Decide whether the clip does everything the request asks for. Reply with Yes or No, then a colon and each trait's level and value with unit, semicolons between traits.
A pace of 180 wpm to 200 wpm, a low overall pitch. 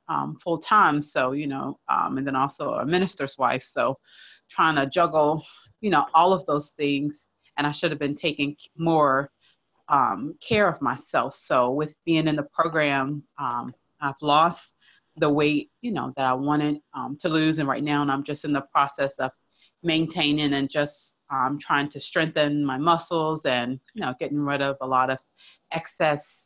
No: average, 185 wpm; medium, 145 Hz